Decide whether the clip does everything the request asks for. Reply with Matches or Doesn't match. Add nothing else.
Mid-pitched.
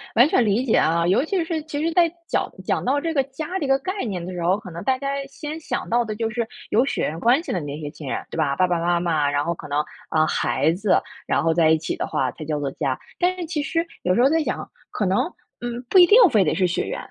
Doesn't match